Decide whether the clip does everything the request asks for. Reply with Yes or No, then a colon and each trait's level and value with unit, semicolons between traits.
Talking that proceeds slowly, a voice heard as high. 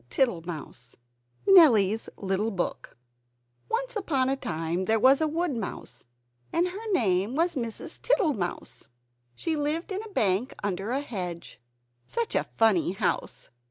Yes: slow, 130 wpm; high, 240 Hz